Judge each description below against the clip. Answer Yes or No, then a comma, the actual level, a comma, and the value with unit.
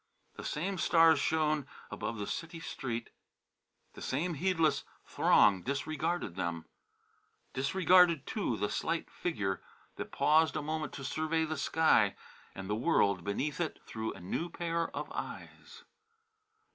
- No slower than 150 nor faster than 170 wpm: No, slow, 135 wpm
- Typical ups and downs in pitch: No, wide, 6.6 semitones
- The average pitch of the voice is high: No, medium, 155 Hz